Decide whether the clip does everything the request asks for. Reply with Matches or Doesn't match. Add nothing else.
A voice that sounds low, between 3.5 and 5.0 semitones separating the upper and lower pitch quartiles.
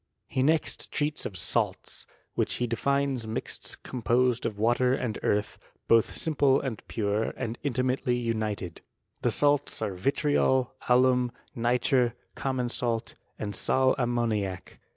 Doesn't match